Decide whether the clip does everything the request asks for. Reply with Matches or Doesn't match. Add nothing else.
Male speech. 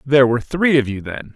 Matches